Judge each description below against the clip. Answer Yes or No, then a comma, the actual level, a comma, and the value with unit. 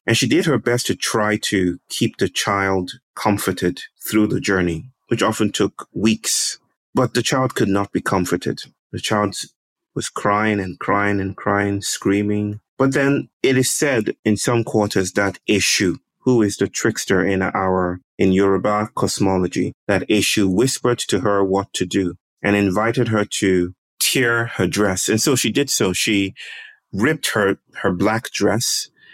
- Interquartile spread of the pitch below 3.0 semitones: No, average, 3.5 semitones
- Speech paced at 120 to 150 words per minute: No, average, 165 wpm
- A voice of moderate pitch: No, low, 100 Hz